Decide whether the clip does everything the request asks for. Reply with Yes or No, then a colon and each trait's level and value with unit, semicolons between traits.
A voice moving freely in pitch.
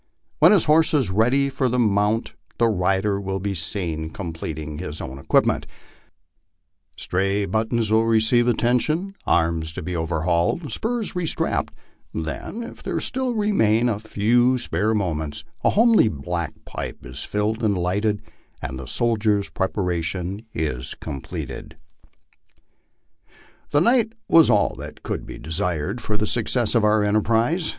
Yes: wide, 5.7 semitones